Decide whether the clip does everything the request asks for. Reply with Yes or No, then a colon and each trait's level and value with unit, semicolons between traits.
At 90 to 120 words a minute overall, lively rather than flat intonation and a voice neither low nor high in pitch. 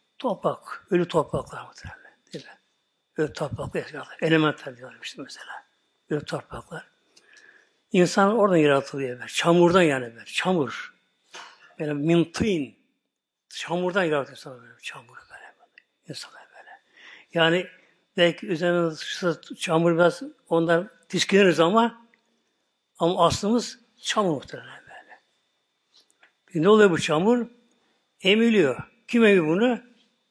Yes: average, 110 wpm; wide, 6.0 semitones; medium, 175 Hz